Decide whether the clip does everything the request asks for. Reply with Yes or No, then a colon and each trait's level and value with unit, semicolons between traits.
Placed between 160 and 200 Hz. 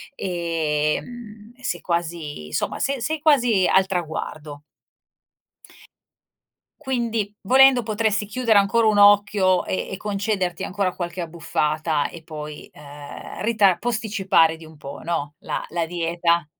Yes: medium, 185 Hz